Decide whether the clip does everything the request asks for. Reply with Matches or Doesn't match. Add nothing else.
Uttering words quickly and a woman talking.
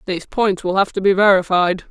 Matches